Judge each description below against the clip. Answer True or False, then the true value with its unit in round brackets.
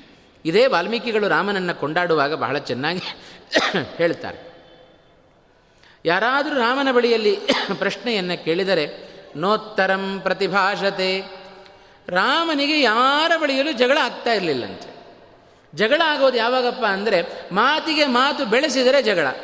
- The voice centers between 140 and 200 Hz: False (225 Hz)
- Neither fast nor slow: True (85 wpm)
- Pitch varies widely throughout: True (5.8 semitones)